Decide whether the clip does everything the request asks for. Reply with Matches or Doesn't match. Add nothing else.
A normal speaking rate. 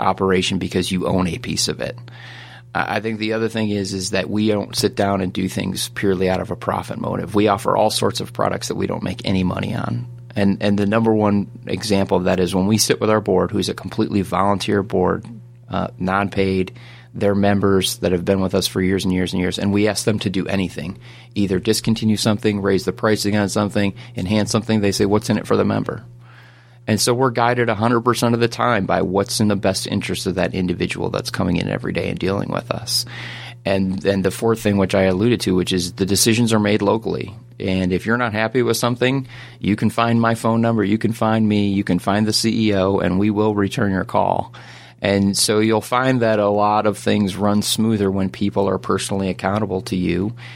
Doesn't match